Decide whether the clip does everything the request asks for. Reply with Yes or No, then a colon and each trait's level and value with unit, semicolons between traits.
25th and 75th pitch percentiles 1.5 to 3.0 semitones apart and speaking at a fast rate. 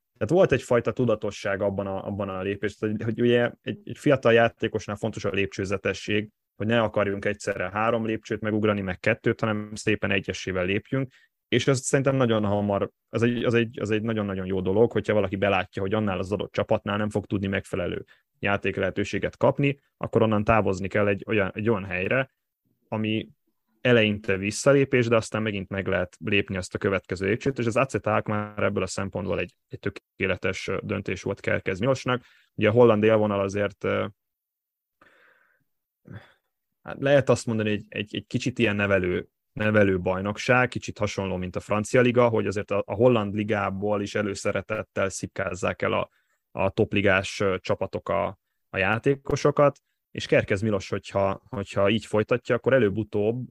Yes: narrow, 2.6 semitones; fast, 160 wpm